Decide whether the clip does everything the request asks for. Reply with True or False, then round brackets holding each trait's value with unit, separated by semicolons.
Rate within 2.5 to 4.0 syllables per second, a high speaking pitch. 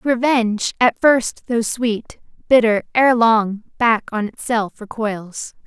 True (3.5 syllables/s; 230 Hz)